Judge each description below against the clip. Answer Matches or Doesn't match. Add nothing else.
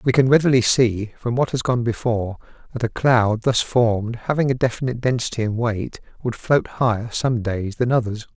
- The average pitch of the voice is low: Matches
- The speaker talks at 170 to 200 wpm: Matches